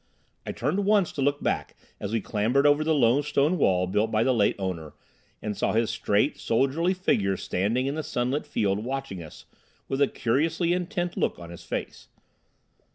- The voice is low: Yes, low, 130 Hz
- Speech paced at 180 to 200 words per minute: Yes, average, 185 wpm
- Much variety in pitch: Yes, wide, 6.5 semitones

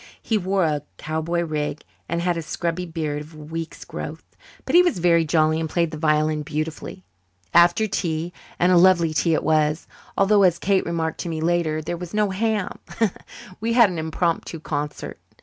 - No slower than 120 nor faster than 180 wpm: No, average, 190 wpm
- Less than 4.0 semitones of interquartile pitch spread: Yes, narrow, 2.4 semitones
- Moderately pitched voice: Yes, medium, 165 Hz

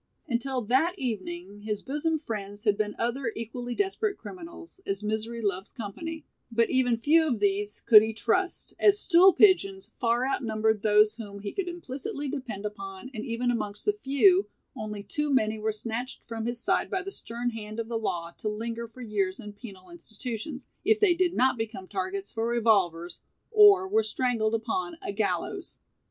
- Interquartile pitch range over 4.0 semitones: Yes, average, 4.7 semitones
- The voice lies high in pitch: Yes, high, 230 Hz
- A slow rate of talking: No, average, 175 wpm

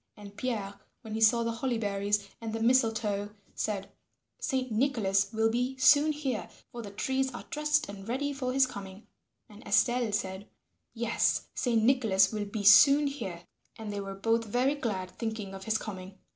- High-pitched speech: Yes, high, 225 Hz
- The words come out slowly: No, average, 175 wpm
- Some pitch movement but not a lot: Yes, average, 4.0 semitones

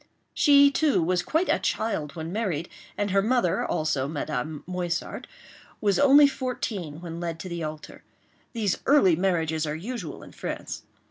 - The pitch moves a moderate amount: No, wide, 6.3 semitones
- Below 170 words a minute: Yes, average, 155 wpm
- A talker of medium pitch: Yes, medium, 180 Hz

